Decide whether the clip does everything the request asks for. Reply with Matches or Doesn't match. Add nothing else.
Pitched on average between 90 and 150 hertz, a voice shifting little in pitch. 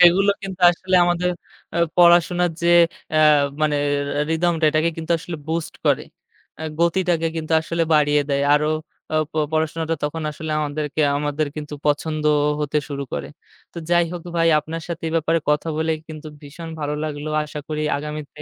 Doesn't match